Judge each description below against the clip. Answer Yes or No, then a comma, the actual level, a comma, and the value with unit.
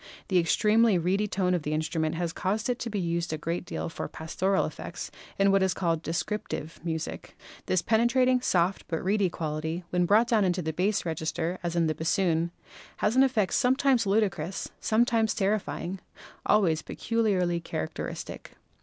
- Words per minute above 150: Yes, average, 175 wpm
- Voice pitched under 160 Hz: No, medium, 185 Hz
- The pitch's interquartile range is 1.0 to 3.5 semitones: No, average, 4.3 semitones